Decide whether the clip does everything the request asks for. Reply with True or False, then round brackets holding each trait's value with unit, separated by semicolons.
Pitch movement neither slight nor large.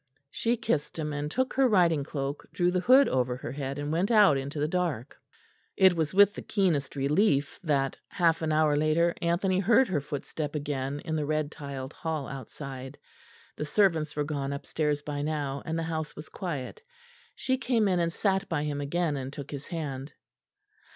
True (3.8 semitones)